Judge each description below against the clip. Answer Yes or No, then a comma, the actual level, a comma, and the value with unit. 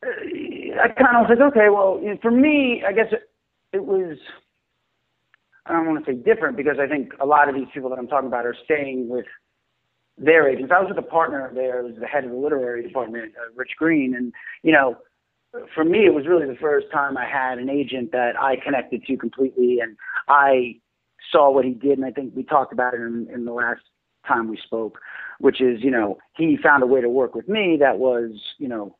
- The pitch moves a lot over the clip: Yes, wide, 7.9 semitones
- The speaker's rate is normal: No, fast, 225 wpm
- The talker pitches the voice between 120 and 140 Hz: Yes, low, 135 Hz